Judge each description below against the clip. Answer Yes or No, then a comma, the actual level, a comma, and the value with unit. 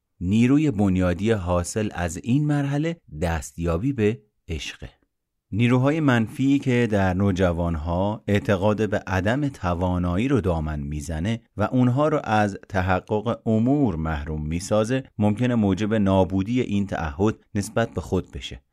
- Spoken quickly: No, average, 120 wpm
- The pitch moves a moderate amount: Yes, average, 4.9 semitones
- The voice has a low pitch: Yes, low, 105 Hz